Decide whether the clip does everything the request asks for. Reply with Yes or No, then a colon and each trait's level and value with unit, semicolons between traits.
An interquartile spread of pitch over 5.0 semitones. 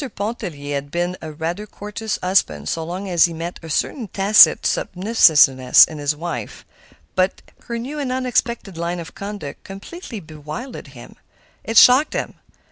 Yes: wide, 5.6 semitones